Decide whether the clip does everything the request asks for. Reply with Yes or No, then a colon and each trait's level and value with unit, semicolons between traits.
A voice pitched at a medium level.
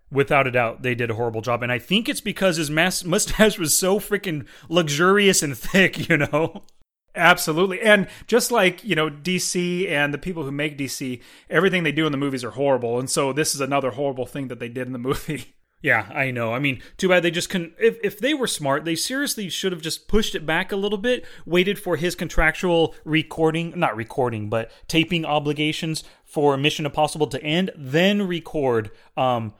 Yes: medium, 160 Hz